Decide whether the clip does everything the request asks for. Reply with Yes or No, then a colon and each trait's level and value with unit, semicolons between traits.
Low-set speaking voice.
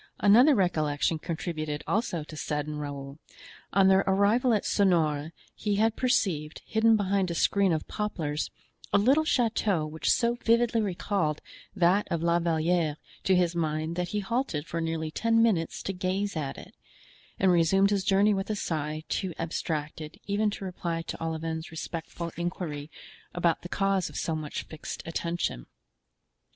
No: medium, 175 Hz